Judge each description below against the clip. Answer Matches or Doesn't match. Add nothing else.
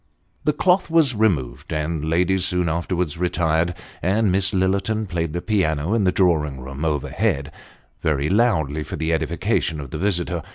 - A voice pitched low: Matches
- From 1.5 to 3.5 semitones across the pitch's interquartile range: Doesn't match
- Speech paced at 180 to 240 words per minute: Doesn't match